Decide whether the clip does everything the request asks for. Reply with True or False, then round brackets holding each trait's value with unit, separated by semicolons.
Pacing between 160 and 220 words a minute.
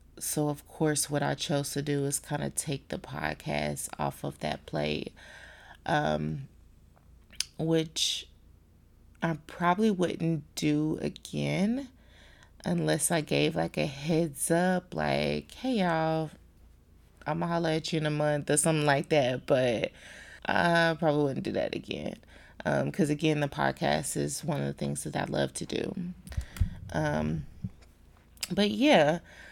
False (145 wpm)